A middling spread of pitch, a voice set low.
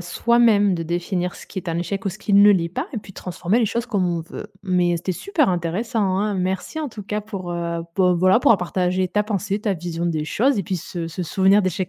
No: average, 3.1 semitones; high, 190 Hz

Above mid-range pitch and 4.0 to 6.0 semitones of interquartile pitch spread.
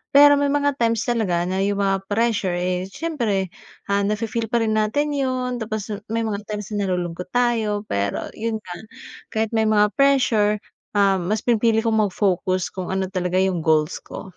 No: high, 210 Hz; average, 3.4 semitones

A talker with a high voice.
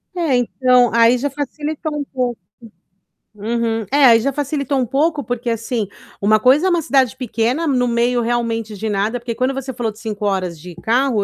Yes: high, 245 Hz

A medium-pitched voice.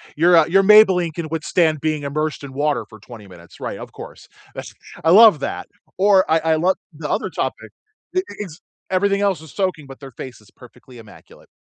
Yes: medium, 160 Hz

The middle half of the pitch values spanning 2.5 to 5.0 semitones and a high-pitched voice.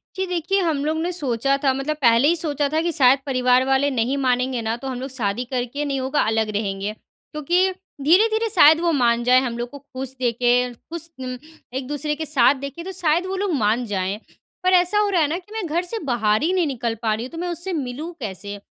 No: wide, 5.5 semitones; very high, 275 Hz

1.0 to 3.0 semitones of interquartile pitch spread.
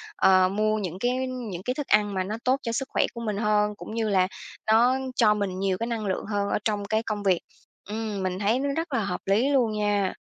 Yes: average, 2.7 semitones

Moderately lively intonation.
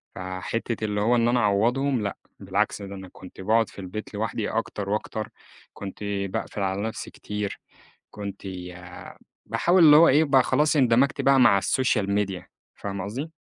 Yes: average, 3.7 semitones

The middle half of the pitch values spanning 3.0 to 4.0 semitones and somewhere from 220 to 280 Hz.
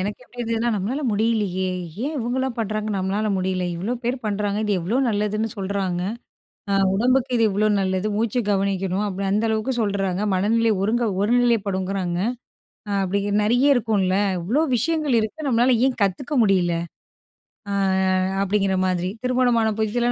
No: average, 3.5 semitones; high, 210 Hz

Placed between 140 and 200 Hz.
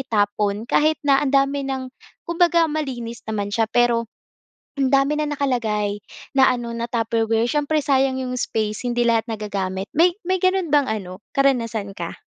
No: high, 245 Hz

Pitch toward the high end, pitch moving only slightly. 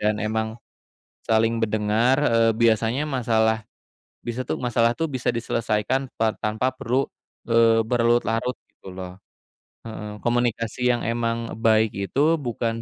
No: low, 115 Hz; narrow, 1.6 semitones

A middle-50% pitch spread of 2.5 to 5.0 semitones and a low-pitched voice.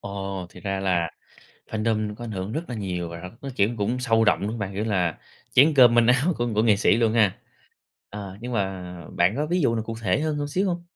Yes: average, 3.9 semitones; low, 110 Hz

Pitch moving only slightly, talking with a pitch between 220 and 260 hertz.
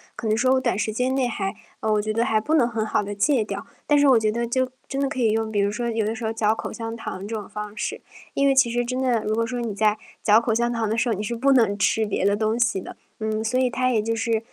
Yes: narrow, 2.2 semitones; high, 225 Hz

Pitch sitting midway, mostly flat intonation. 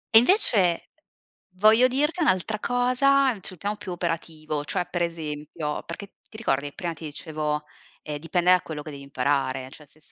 No: medium, 170 Hz; wide, 6.1 semitones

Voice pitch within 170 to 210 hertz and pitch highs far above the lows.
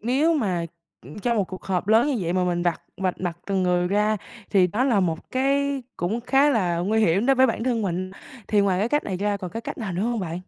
No: high, 200 Hz; average, 4.8 semitones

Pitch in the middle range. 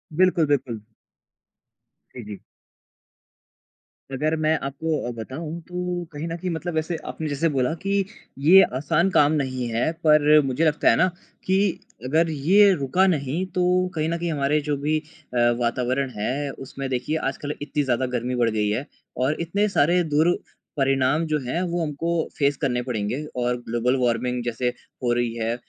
Yes: medium, 145 Hz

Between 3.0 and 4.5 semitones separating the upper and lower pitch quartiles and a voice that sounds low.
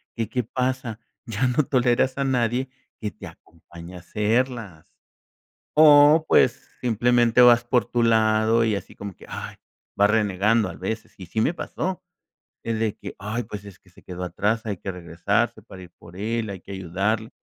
Yes: average, 3.7 semitones; low, 110 Hz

